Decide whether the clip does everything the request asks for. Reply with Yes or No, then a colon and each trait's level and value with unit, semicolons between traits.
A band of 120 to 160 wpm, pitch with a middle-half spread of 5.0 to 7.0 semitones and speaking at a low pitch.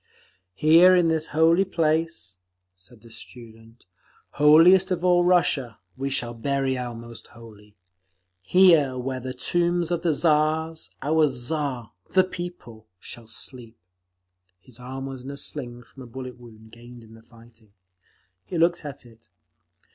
Yes: average, 145 wpm; wide, 5.6 semitones; low, 130 Hz